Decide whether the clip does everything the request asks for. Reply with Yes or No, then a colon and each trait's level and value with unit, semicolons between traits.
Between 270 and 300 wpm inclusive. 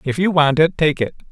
Yes: fast, 275 wpm